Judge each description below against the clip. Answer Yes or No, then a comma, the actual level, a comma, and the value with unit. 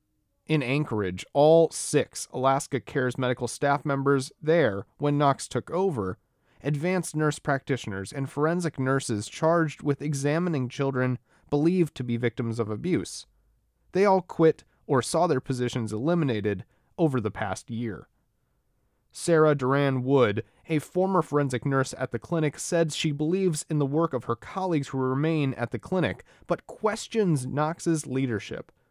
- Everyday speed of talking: Yes, average, 145 wpm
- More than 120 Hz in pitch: Yes, medium, 140 Hz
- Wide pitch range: No, average, 4.3 semitones